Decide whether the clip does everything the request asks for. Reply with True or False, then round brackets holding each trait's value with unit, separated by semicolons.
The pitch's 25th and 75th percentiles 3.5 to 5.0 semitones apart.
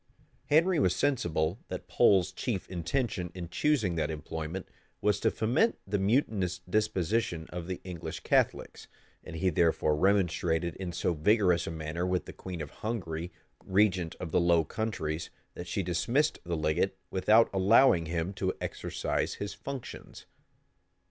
True (4.1 semitones)